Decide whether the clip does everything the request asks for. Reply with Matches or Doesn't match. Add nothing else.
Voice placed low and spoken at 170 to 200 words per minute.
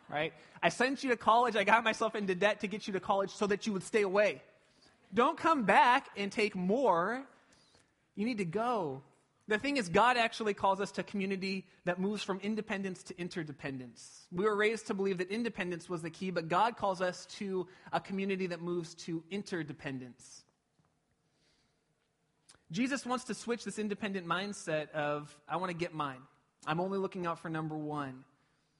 Doesn't match